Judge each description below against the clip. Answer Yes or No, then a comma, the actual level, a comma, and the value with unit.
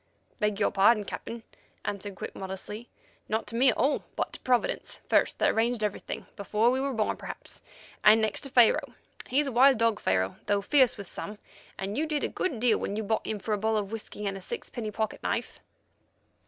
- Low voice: No, high, 220 Hz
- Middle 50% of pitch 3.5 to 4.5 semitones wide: No, average, 3.1 semitones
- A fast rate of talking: Yes, fast, 210 wpm